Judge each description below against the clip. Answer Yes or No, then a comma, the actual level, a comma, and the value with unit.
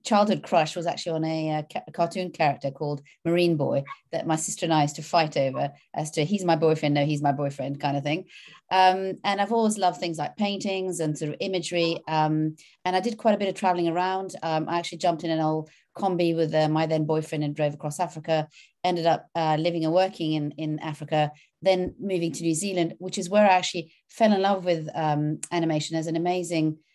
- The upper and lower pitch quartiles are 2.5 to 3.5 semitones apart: Yes, average, 2.8 semitones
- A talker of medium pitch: Yes, medium, 165 Hz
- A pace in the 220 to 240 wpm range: Yes, fast, 225 wpm